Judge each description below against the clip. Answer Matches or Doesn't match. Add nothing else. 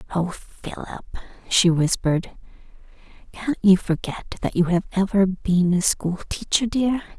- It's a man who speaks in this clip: Doesn't match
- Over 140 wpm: Doesn't match